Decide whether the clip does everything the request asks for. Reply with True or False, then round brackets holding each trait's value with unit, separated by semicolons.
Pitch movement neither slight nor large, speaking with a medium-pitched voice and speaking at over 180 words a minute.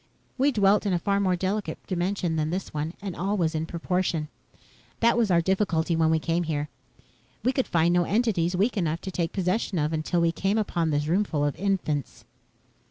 True (3.6 semitones; 175 Hz; 200 wpm)